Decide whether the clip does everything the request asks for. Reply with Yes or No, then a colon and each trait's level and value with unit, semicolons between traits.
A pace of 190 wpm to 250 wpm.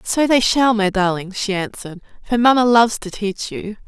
Yes: average, 200 wpm